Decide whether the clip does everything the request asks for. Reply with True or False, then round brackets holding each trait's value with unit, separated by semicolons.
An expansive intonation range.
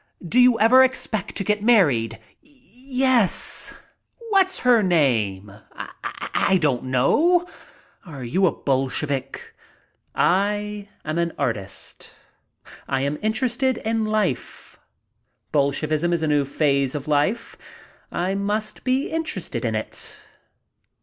True (8.8 semitones)